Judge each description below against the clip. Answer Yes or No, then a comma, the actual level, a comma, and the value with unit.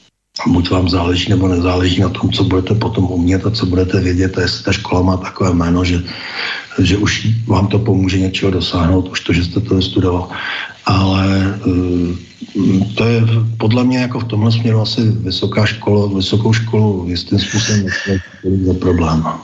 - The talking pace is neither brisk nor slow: No, fast, 175 wpm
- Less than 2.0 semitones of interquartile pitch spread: No, average, 2.7 semitones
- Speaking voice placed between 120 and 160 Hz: No, very low, 95 Hz